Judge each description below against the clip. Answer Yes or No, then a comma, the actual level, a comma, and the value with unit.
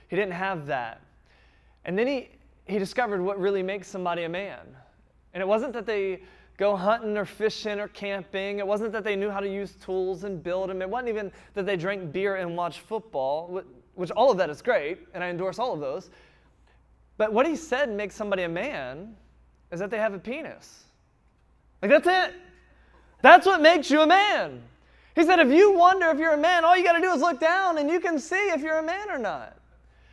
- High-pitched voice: Yes, high, 205 Hz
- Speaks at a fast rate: Yes, fast, 215 wpm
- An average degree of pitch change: No, wide, 8.3 semitones